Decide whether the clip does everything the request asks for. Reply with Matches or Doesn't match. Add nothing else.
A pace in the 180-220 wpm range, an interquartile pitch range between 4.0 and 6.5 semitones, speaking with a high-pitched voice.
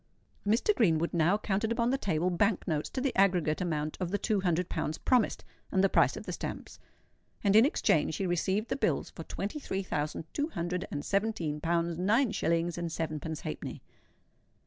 Doesn't match